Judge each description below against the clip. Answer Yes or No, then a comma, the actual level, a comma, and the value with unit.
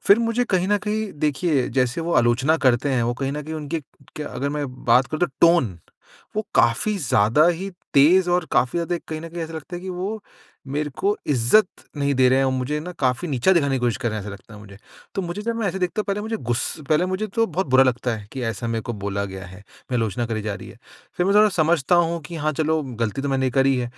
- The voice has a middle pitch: Yes, medium, 150 Hz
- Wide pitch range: Yes, wide, 6.4 semitones